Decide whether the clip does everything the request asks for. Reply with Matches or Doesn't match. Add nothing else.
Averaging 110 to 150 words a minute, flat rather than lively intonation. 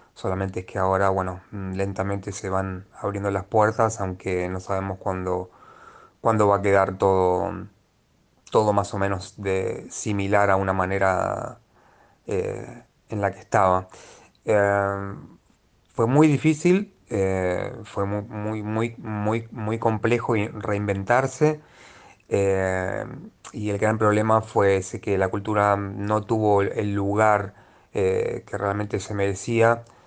Matches